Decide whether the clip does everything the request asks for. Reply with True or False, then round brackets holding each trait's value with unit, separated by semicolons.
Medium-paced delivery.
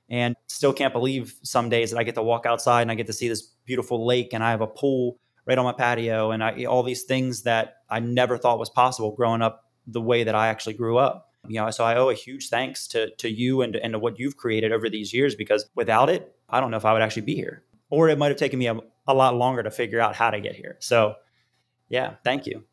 False (270 wpm)